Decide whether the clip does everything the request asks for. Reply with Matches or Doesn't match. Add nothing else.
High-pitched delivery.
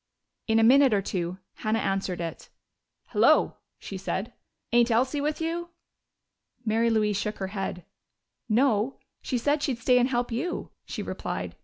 Matches